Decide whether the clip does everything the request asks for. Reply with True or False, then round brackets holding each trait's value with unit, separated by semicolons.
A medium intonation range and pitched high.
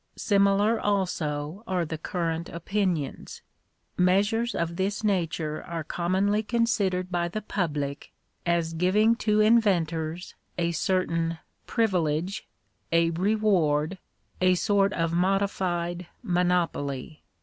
False (3.3 semitones; 180 Hz)